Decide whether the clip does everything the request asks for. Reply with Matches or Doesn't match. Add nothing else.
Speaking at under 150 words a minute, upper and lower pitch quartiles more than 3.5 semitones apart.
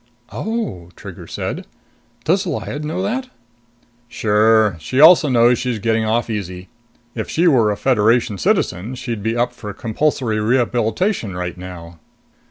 Matches